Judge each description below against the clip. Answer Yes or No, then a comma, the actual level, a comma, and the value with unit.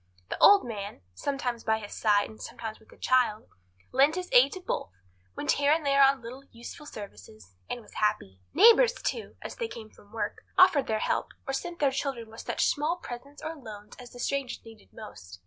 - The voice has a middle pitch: No, high, 245 Hz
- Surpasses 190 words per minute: Yes, fast, 205 wpm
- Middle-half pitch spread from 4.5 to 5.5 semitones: Yes, average, 4.9 semitones